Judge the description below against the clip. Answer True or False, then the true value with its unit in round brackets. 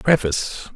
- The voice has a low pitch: True (120 Hz)